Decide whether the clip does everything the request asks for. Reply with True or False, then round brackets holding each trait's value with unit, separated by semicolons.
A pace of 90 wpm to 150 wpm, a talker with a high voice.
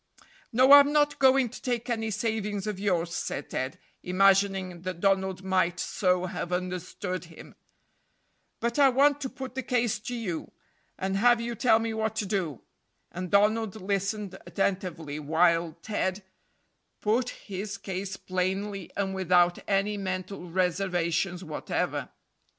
True (140 wpm; 195 Hz)